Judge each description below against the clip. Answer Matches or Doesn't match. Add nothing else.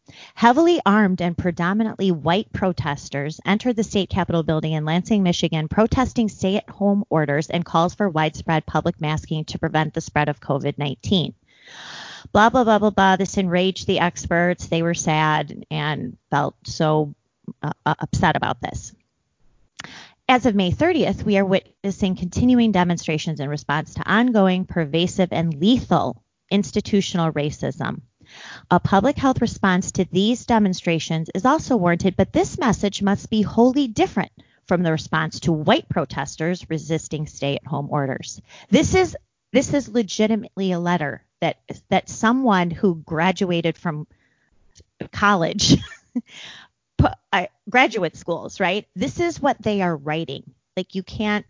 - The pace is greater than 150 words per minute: Doesn't match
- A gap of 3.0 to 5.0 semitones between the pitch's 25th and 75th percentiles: Matches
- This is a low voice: Doesn't match